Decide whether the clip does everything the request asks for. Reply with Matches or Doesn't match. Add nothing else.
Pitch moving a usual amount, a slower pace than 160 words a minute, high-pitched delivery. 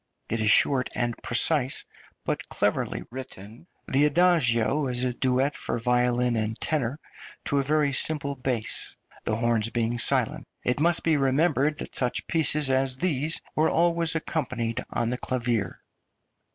Doesn't match